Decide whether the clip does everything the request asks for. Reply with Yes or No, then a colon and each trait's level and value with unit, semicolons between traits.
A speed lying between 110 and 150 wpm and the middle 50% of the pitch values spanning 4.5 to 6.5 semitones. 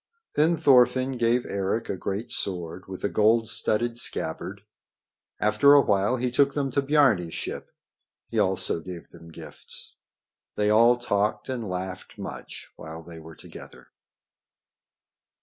Yes: average, 140 wpm; average, 5.2 semitones